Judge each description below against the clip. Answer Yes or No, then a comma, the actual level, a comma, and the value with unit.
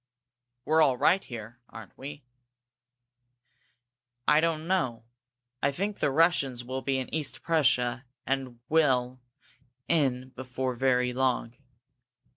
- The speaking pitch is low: Yes, low, 130 Hz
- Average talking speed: No, slow, 115 wpm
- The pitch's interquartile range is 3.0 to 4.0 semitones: Yes, average, 3.7 semitones